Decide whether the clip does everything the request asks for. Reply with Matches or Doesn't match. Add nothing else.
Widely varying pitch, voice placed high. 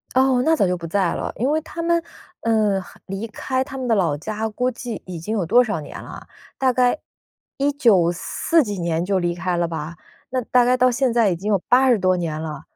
Matches